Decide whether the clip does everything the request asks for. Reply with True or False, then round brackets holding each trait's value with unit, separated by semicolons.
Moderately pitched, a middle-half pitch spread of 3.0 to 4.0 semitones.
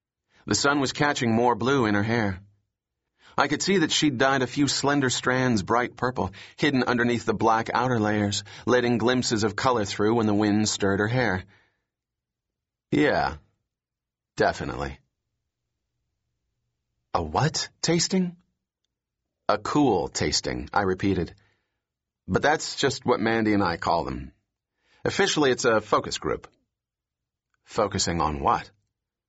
False (115 Hz; 3.7 semitones)